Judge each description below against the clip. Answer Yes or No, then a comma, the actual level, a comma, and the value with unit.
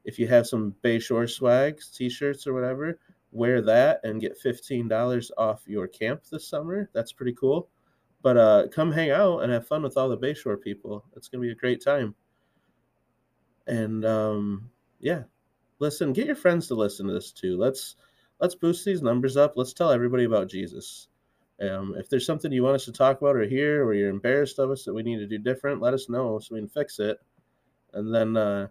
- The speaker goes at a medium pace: No, fast, 210 wpm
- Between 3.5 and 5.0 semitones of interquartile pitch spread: Yes, average, 4.3 semitones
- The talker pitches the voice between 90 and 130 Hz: Yes, low, 125 Hz